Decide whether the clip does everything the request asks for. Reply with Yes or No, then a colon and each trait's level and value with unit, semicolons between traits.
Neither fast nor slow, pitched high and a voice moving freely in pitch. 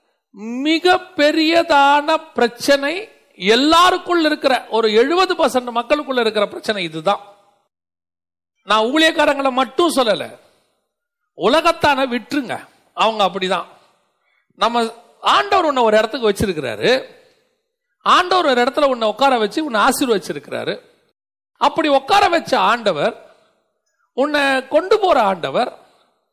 Yes: average, 90 wpm; very high, 280 Hz; wide, 6.8 semitones